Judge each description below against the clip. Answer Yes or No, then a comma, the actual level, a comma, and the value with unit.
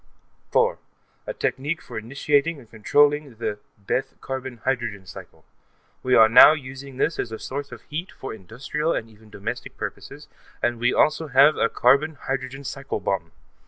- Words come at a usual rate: Yes, average, 160 wpm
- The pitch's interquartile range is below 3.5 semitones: No, average, 4.0 semitones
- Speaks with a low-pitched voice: Yes, low, 130 Hz